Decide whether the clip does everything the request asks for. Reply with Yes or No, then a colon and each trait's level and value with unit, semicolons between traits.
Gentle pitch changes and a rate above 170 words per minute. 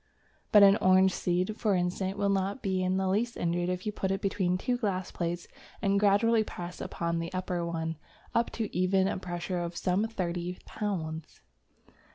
Yes: narrow, 2.3 semitones; average, 185 wpm